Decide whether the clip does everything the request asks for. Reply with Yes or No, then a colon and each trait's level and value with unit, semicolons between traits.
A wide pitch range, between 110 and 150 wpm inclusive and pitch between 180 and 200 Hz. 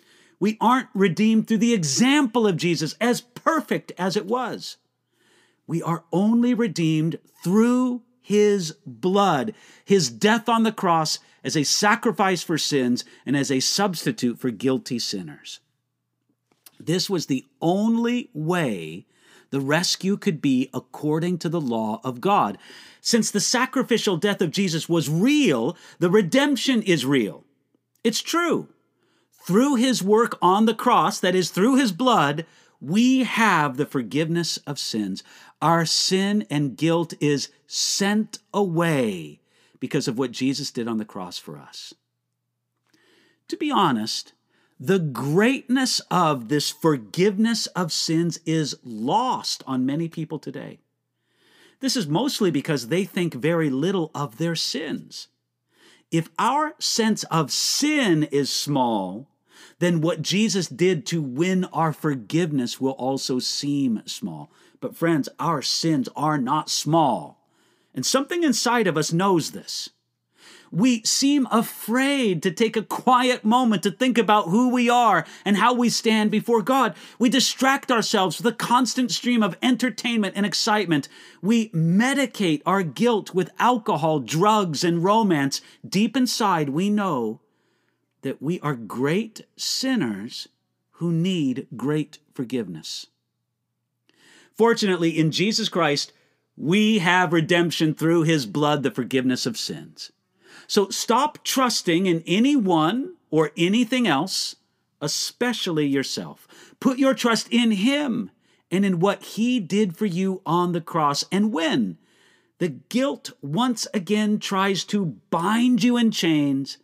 Yes: wide, 6.8 semitones; slow, 135 wpm; high, 190 Hz